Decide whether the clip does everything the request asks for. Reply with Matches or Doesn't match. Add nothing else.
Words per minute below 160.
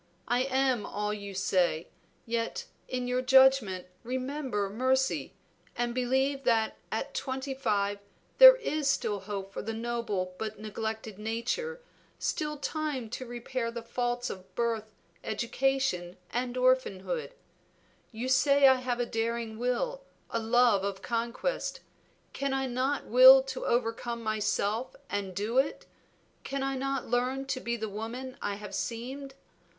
Matches